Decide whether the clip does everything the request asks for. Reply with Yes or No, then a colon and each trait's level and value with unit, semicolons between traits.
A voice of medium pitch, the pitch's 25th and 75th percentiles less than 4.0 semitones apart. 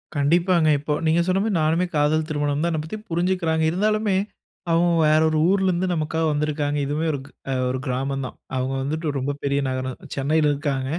Yes: medium, 155 Hz; average, 3.3 semitones